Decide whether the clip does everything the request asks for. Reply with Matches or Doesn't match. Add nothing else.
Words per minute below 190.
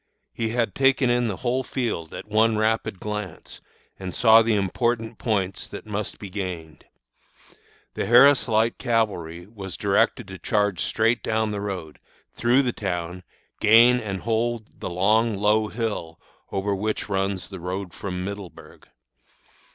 Matches